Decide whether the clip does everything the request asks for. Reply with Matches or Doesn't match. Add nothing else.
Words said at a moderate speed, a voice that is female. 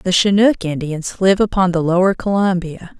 Matches